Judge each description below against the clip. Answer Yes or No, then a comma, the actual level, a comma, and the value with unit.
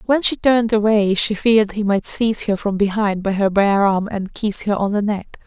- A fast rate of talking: Yes, fast, 240 wpm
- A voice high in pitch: Yes, high, 205 Hz